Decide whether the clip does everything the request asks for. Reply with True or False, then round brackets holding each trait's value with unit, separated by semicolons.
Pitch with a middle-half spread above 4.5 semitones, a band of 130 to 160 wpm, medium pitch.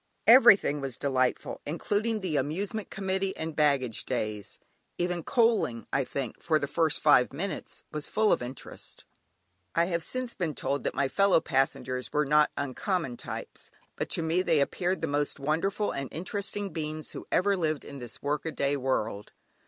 False (5.5 semitones; 170 wpm; 155 Hz)